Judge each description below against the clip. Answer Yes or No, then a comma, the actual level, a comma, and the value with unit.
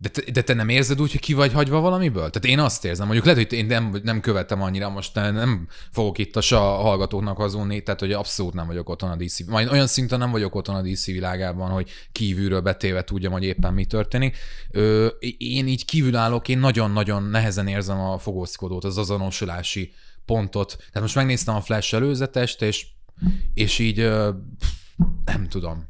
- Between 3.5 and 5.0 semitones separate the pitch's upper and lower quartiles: Yes, average, 3.9 semitones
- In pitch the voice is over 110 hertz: No, low, 105 Hz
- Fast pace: Yes, fast, 195 wpm